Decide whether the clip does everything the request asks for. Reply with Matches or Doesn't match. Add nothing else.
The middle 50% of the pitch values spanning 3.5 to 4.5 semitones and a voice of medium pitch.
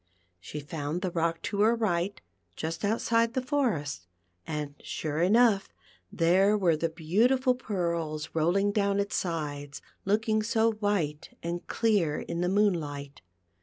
Doesn't match